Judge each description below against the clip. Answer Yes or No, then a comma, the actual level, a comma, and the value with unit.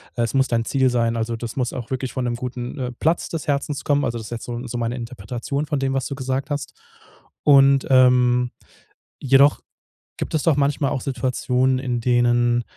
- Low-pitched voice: Yes, low, 125 Hz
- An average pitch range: No, narrow, 2.3 semitones